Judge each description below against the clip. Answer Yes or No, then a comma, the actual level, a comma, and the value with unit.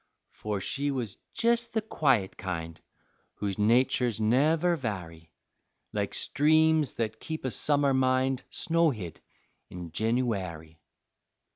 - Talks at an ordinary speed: No, slow, 110 wpm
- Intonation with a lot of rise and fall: Yes, wide, 7.1 semitones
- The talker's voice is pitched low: Yes, low, 125 Hz